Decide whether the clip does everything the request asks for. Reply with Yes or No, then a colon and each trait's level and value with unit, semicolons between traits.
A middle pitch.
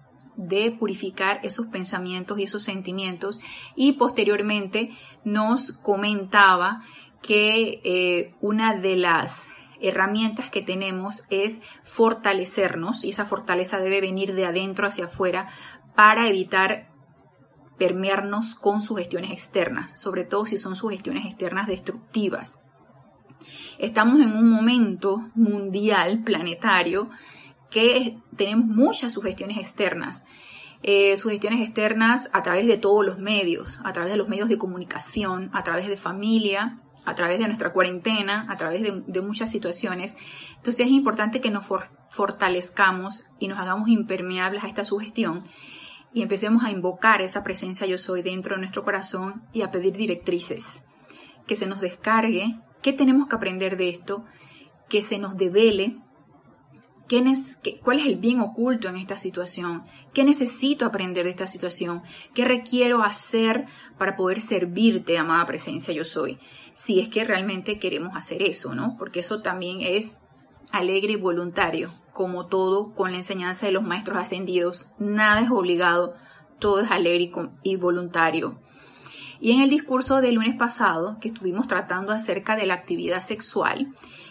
No: high, 200 Hz